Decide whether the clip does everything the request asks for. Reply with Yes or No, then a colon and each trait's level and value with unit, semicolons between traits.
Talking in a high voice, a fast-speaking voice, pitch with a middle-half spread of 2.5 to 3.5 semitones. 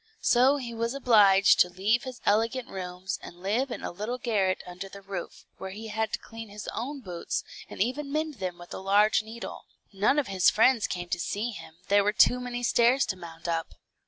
No: high, 210 Hz; fast, 215 wpm; average, 4.3 semitones